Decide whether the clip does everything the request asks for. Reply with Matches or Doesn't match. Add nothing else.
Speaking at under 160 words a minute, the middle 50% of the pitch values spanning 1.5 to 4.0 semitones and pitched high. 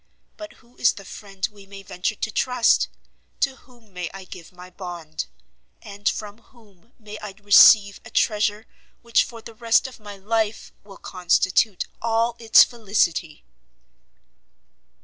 Matches